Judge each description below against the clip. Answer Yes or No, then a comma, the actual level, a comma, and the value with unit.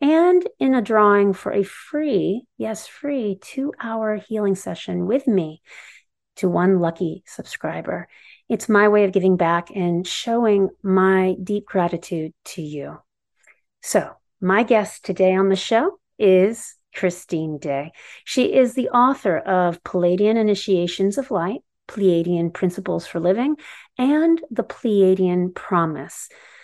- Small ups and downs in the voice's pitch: No, average, 4.5 semitones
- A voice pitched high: Yes, high, 195 Hz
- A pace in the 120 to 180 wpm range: Yes, slow, 135 wpm